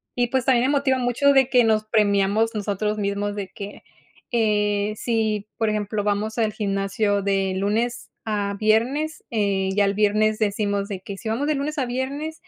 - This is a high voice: Yes, high, 215 Hz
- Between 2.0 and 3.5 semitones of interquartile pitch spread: Yes, average, 3.0 semitones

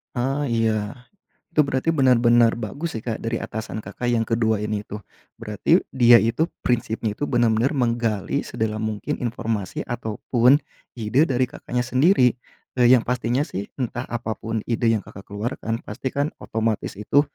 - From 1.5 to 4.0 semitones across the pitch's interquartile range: Yes, narrow, 2.5 semitones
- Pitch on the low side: Yes, low, 115 Hz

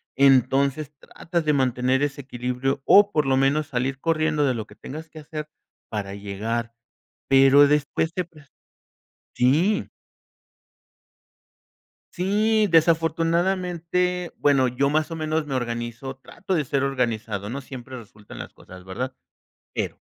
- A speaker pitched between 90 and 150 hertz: Yes, medium, 140 Hz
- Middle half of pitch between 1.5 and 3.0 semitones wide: No, average, 4.3 semitones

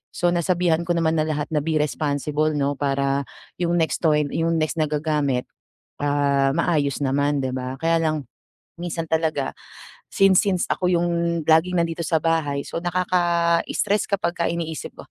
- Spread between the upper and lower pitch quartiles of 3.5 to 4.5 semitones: No, average, 2.9 semitones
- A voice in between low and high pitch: Yes, medium, 160 Hz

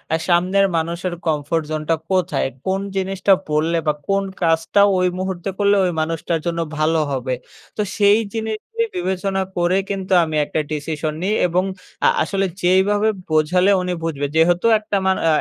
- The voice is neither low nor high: Yes, medium, 180 Hz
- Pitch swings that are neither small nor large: Yes, average, 3.2 semitones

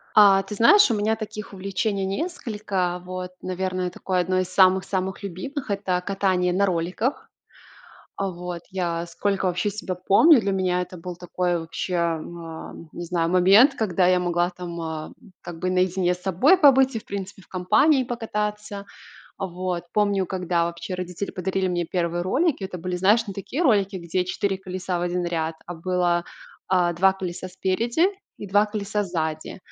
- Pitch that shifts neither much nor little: No, narrow, 2.2 semitones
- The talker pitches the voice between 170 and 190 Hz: Yes, medium, 185 Hz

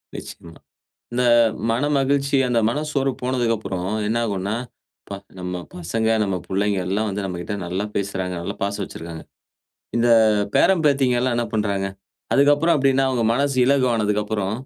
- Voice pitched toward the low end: Yes, low, 110 Hz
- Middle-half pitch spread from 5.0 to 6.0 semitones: Yes, wide, 5.4 semitones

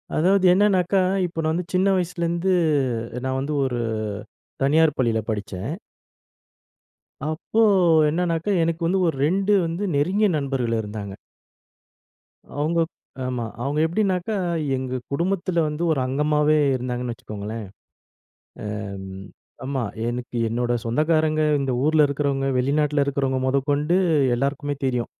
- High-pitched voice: No, medium, 145 Hz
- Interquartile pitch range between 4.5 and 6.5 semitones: Yes, average, 4.8 semitones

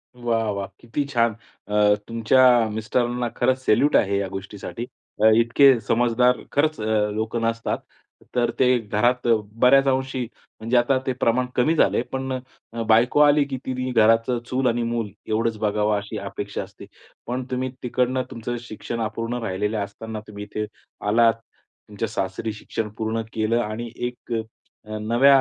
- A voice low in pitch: Yes, low, 115 Hz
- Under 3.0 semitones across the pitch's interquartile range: Yes, narrow, 2.6 semitones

